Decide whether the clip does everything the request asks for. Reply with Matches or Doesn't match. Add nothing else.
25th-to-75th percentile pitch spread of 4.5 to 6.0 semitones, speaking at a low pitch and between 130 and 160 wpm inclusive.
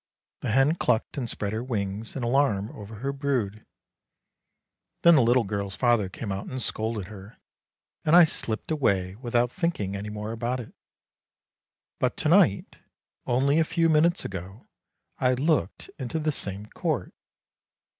Matches